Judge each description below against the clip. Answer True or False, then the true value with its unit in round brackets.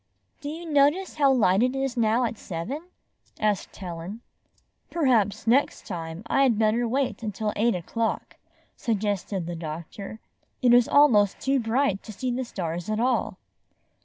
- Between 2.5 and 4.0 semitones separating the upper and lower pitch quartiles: False (4.8 semitones)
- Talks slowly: False (155 wpm)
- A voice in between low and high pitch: False (225 Hz)